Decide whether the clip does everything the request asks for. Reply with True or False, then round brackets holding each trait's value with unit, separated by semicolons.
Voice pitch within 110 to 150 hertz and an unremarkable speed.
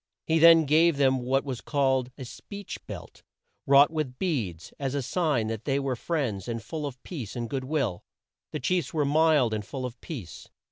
True (135 Hz; 195 wpm)